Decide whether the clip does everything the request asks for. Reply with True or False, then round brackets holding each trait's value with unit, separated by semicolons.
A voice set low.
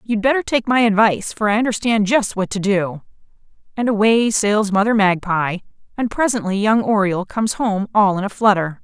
False (210 Hz)